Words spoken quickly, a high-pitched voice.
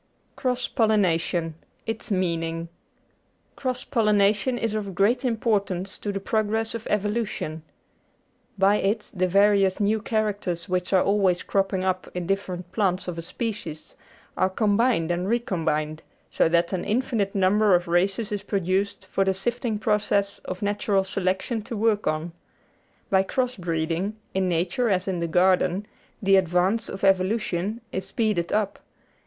No: average, 145 wpm; high, 195 Hz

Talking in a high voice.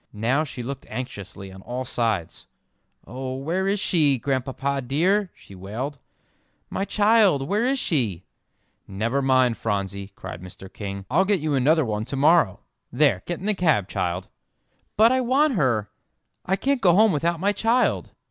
No: medium, 140 Hz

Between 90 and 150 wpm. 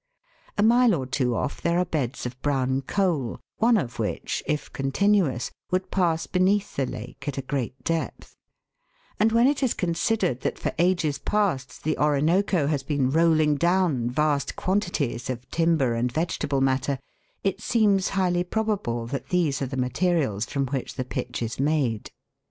No: average, 165 wpm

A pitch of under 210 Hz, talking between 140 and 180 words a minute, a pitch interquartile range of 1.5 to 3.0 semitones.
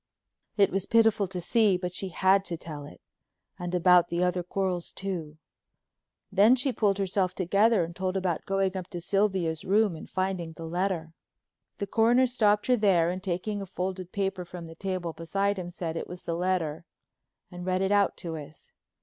No: medium, 185 Hz; average, 190 wpm; narrow, 2.4 semitones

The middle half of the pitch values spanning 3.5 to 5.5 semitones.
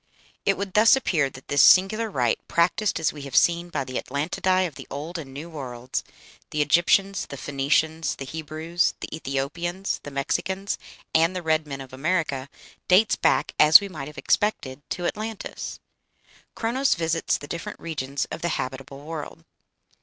Yes: average, 4.8 semitones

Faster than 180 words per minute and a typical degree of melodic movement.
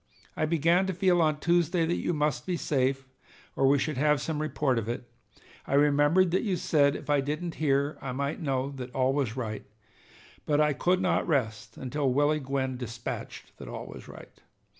Yes: average, 190 wpm; average, 3.3 semitones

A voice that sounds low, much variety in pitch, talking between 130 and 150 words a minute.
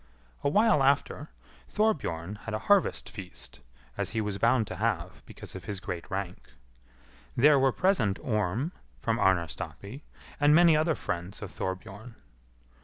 Yes: low, 110 Hz; wide, 7.2 semitones; average, 145 wpm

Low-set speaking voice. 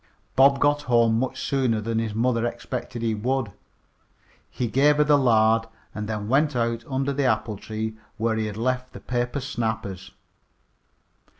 Yes: low, 120 Hz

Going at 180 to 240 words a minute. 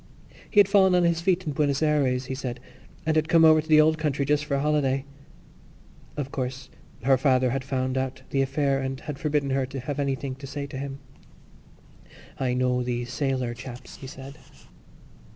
Yes: average, 195 wpm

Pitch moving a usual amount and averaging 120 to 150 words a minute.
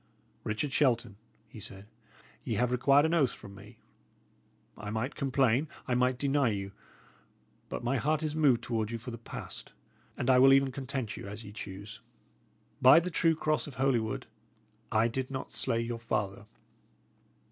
No: average, 3.7 semitones; average, 170 wpm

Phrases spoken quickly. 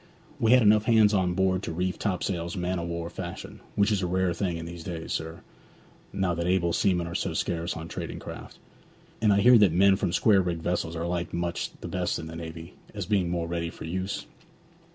Yes: fast, 215 wpm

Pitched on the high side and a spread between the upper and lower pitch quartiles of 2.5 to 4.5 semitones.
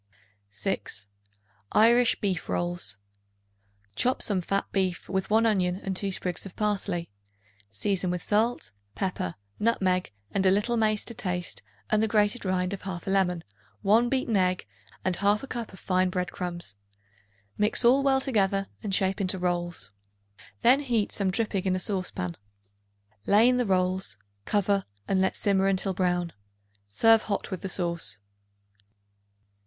Yes: high, 195 Hz; average, 2.8 semitones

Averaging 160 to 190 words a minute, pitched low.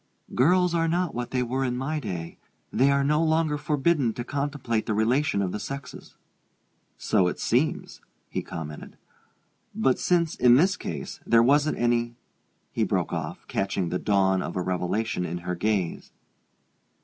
Yes: average, 165 wpm; low, 125 Hz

